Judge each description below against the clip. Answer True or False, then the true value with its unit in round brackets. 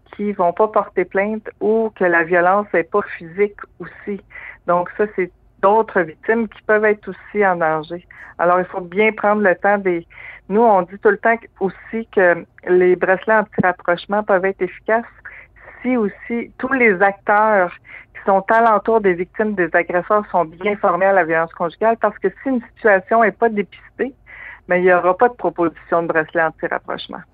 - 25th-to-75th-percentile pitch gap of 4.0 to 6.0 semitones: False (3.3 semitones)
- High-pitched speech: True (195 Hz)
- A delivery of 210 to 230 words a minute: False (185 wpm)